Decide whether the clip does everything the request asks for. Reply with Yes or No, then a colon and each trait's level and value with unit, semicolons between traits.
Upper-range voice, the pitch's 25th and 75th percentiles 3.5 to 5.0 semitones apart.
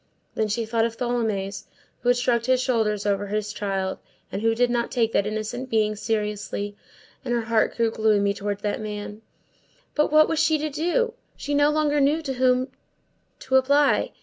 Yes: high, 230 Hz; average, 3.9 semitones